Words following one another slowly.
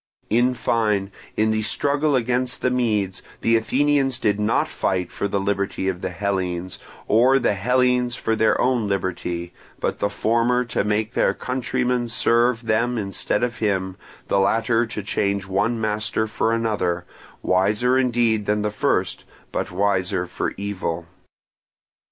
No: average, 150 wpm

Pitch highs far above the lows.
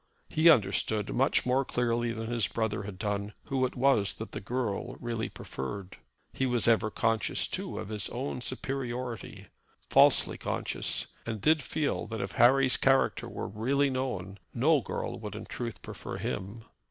No: average, 3.6 semitones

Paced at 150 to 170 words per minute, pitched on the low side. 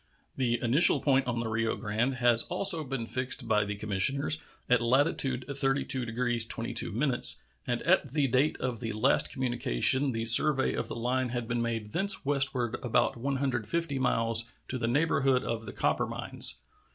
Yes: average, 165 wpm; low, 125 Hz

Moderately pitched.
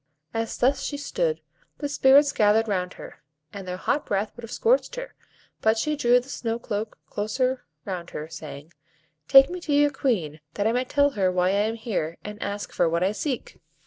No: high, 225 Hz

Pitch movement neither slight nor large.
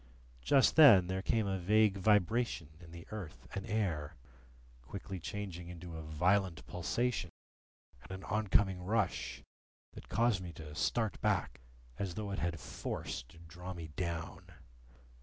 Yes: average, 3.6 semitones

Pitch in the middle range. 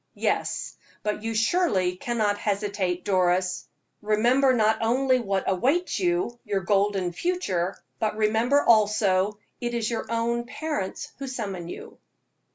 No: high, 215 Hz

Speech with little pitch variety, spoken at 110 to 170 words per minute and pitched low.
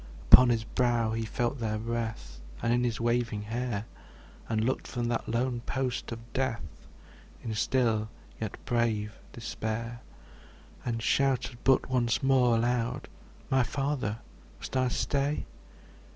Yes: narrow, 2.1 semitones; slow, 135 wpm; low, 120 Hz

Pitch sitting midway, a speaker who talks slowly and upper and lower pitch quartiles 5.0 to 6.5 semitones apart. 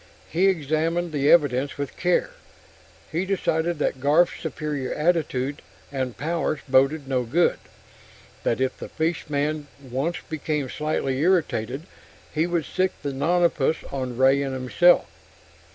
No: medium, 150 Hz; slow, 130 wpm; average, 3.8 semitones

